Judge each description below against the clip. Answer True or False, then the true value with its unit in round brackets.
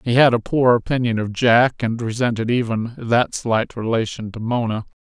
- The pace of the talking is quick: False (180 wpm)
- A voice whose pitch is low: True (115 Hz)